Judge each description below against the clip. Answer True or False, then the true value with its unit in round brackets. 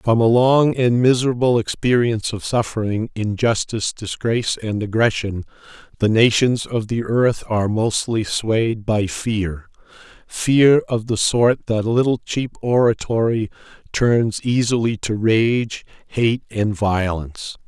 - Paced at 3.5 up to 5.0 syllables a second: True (4.2 syllables/s)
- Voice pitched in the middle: False (115 Hz)